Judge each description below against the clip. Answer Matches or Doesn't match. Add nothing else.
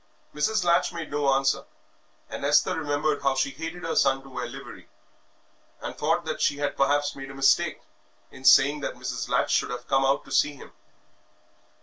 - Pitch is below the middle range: Doesn't match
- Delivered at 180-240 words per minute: Matches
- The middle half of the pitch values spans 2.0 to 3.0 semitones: Matches